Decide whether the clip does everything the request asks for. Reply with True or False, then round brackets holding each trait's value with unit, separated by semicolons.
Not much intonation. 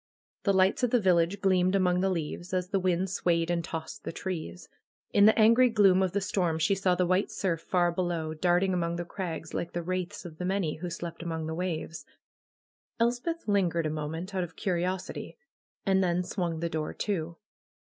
True (2.3 semitones)